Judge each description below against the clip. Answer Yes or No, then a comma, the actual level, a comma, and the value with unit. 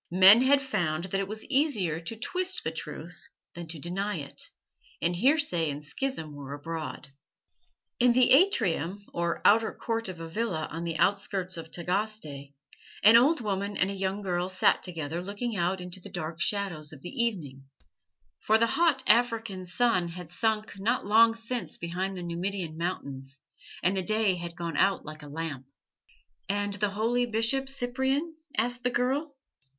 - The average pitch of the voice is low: No, high, 195 Hz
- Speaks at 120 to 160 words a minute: No, average, 170 wpm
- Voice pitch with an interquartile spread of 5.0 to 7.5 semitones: Yes, average, 5.3 semitones